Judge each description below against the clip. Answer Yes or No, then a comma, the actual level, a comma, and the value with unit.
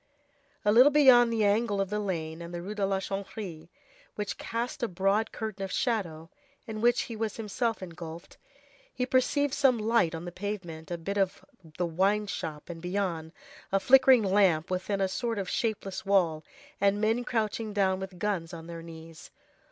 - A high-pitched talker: Yes, high, 200 Hz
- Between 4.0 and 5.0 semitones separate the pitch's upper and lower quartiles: Yes, average, 4.3 semitones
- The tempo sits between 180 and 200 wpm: Yes, average, 185 wpm